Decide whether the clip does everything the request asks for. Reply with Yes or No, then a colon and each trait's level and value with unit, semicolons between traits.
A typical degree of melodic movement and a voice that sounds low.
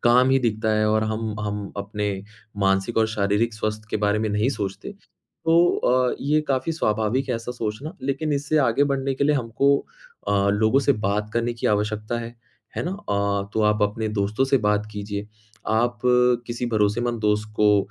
Yes: average, 3.6 semitones; low, 110 Hz